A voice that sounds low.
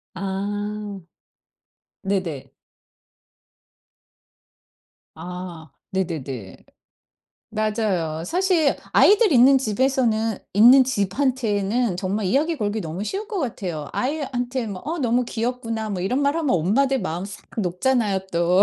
No: high, 215 Hz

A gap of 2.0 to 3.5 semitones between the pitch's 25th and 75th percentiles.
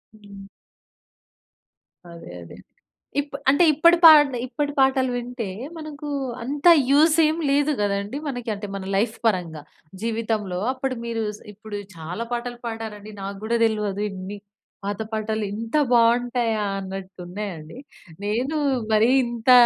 No: average, 4.3 semitones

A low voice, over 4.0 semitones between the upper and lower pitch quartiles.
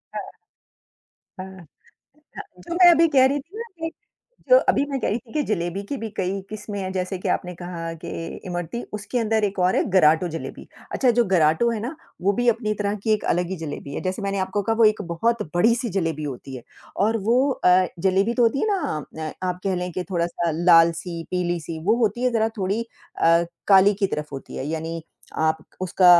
No: high, 190 Hz; average, 4.9 semitones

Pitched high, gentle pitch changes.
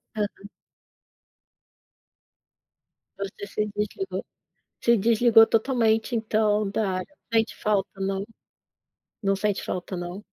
Yes: high, 210 Hz; narrow, 2.2 semitones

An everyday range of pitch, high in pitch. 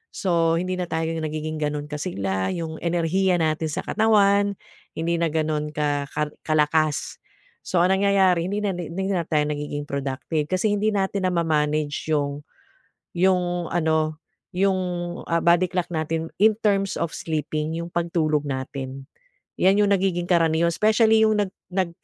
No: average, 3.6 semitones; medium, 165 Hz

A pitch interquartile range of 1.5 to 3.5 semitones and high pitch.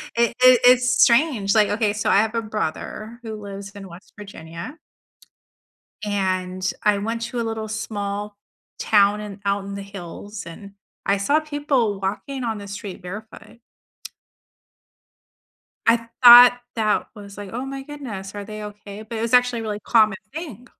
Yes: average, 2.8 semitones; high, 210 Hz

